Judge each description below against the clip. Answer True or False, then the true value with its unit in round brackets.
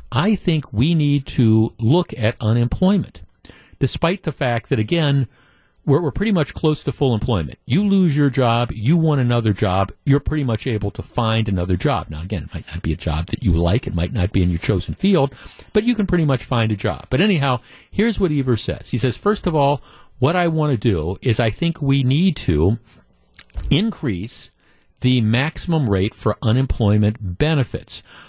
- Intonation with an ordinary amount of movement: False (6.2 semitones)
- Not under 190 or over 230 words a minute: True (195 wpm)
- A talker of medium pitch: False (125 Hz)